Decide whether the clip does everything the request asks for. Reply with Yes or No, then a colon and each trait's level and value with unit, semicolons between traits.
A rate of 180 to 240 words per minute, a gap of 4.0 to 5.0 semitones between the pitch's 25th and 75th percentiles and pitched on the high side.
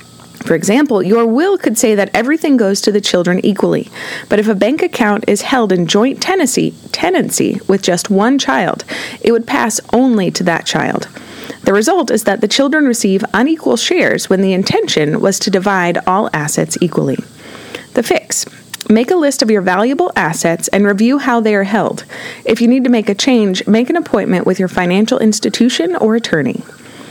Yes: average, 185 wpm; average, 4.4 semitones; high, 220 Hz